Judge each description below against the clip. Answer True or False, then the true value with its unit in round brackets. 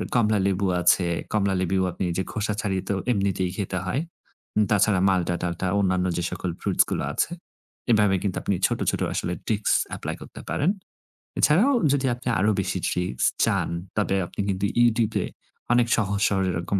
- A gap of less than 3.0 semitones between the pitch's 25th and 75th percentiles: True (2.5 semitones)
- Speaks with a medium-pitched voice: False (100 Hz)